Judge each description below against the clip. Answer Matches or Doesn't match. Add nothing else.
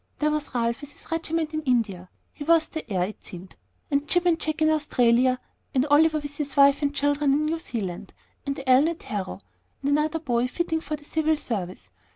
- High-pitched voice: Matches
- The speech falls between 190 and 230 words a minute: Matches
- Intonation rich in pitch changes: Doesn't match